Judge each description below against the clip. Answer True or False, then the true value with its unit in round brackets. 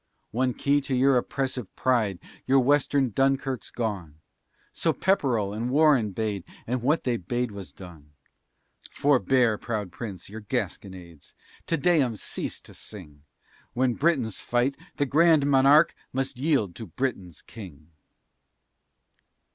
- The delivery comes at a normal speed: False (130 wpm)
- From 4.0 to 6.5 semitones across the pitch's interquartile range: True (5.2 semitones)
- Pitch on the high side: False (125 Hz)